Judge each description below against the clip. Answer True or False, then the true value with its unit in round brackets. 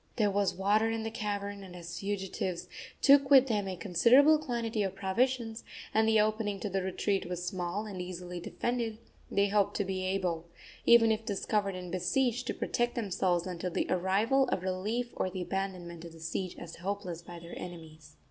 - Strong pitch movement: False (3.6 semitones)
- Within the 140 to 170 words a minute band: False (190 wpm)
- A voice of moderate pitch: False (195 Hz)